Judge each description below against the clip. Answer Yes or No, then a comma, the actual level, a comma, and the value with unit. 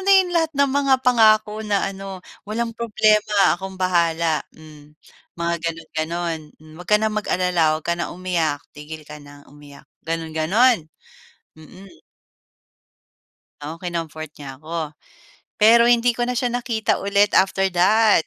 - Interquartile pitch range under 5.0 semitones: No, wide, 5.5 semitones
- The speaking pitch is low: No, medium, 185 Hz